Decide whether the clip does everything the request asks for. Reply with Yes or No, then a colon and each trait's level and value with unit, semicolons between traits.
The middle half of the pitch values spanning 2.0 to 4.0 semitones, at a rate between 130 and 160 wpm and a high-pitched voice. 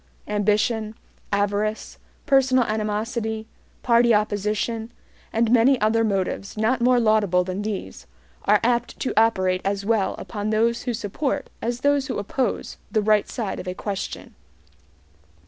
Yes: narrow, 2.4 semitones; slow, 135 wpm; high, 220 Hz